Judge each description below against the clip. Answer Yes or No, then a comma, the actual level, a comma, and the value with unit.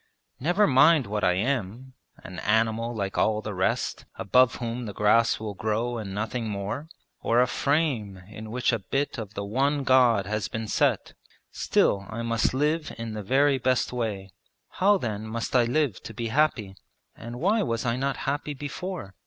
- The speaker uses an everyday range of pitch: Yes, average, 4.1 semitones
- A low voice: Yes, low, 115 Hz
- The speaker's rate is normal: Yes, average, 180 wpm